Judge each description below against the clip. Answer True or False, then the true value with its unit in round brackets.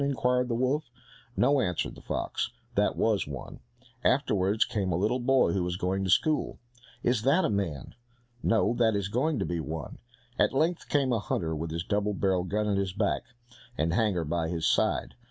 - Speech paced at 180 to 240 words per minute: True (190 wpm)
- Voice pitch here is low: True (100 Hz)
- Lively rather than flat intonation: True (5.8 semitones)